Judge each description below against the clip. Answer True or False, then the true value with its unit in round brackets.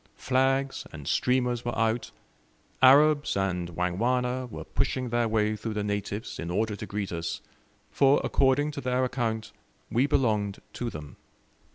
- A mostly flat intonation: False (4.0 semitones)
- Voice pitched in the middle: False (115 Hz)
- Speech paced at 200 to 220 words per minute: False (150 wpm)